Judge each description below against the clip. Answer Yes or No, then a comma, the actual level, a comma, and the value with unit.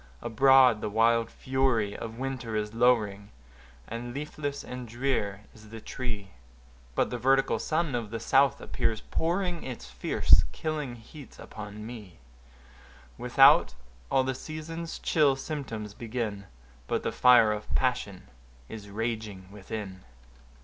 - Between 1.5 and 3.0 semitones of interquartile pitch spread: No, average, 4.0 semitones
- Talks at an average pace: No, slow, 130 wpm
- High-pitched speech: No, low, 115 Hz